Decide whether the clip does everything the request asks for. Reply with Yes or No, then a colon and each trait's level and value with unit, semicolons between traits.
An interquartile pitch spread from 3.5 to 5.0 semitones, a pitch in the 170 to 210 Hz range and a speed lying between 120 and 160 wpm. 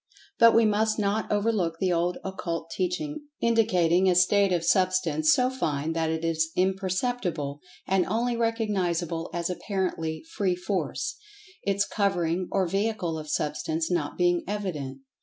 Yes: average, 4.0 semitones; medium, 185 Hz; average, 145 wpm